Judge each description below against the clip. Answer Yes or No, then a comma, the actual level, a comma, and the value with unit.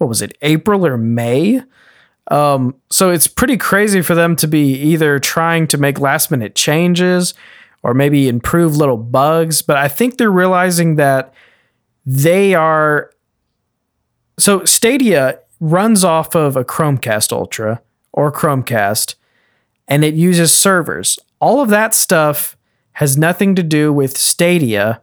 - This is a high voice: No, medium, 155 Hz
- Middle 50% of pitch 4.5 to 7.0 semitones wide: Yes, average, 4.9 semitones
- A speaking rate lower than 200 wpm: Yes, average, 140 wpm